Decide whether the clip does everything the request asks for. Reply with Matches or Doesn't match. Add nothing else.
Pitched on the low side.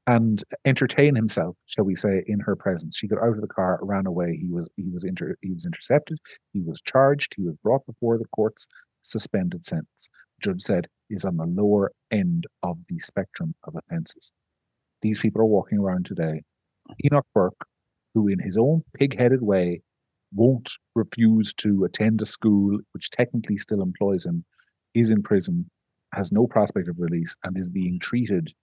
Matches